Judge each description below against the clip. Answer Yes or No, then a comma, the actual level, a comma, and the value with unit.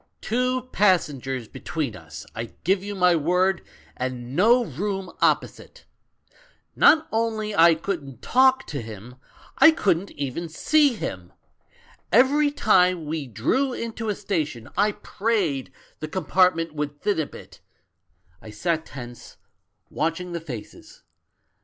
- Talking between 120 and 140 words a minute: Yes, slow, 135 wpm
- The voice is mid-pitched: Yes, medium, 175 Hz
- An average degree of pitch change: No, wide, 7.1 semitones